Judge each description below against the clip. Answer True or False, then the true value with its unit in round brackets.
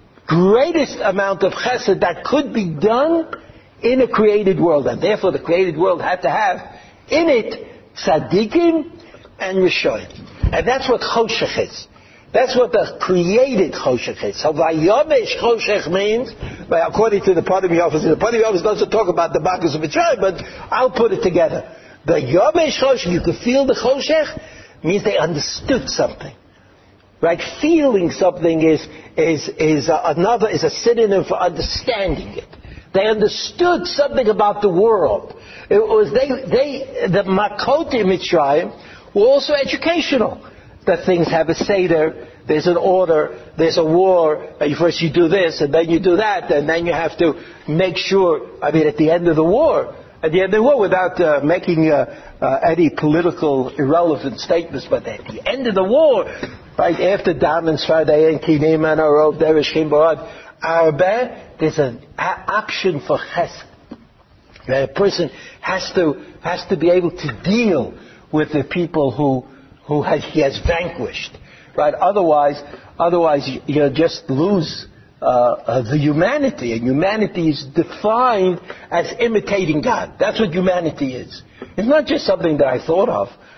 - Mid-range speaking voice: True (180 Hz)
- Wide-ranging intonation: True (6.8 semitones)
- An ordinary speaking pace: True (165 wpm)